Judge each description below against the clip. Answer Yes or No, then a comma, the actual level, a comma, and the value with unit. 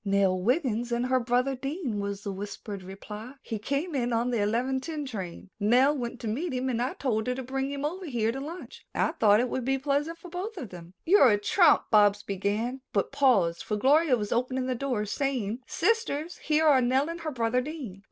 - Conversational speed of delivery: No, fast, 220 wpm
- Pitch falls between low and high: No, very high, 250 Hz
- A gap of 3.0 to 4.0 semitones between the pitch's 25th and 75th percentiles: No, average, 4.8 semitones